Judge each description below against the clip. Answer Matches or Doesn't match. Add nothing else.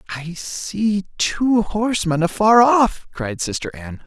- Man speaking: Matches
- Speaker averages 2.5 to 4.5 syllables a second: Matches